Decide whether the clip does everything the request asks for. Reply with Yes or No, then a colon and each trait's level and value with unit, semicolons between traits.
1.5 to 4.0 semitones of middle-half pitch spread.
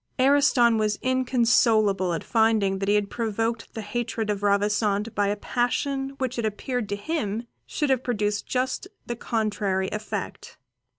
Yes: average, 3.2 semitones